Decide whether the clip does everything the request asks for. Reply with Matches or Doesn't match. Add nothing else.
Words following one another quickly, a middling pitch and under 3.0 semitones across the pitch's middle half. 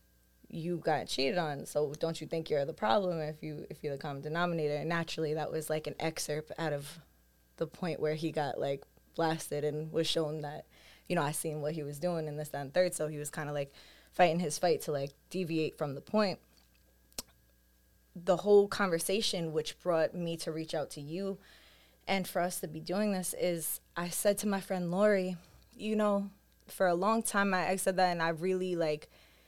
Doesn't match